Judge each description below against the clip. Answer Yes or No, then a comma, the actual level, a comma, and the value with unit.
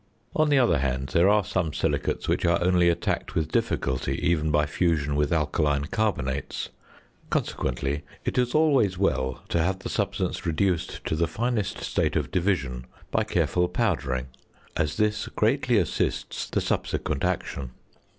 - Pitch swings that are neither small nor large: No, wide, 5.8 semitones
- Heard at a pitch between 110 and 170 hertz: No, very low, 85 Hz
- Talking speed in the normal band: Yes, average, 150 wpm